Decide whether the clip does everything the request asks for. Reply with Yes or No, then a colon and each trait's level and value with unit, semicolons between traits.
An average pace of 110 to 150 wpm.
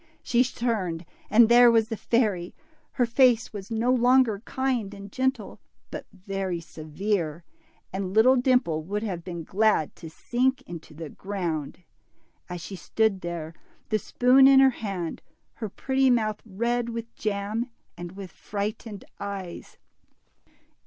Yes: average, 140 wpm